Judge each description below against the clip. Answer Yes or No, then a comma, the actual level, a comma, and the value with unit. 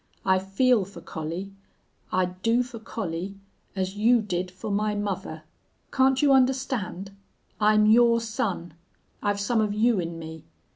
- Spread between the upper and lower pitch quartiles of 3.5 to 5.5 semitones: Yes, average, 3.9 semitones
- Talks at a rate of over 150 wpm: No, average, 145 wpm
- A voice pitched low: No, high, 205 Hz